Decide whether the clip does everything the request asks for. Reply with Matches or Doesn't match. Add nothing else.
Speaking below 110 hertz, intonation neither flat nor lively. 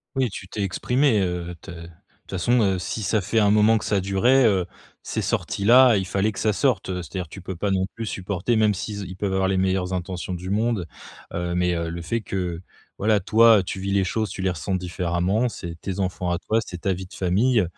Matches